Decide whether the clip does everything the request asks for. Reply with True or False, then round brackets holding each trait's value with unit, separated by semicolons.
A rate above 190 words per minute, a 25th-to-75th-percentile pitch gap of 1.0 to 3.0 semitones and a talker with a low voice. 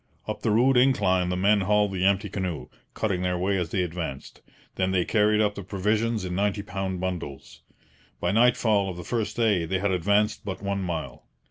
True (200 wpm; 2.5 semitones; 95 Hz)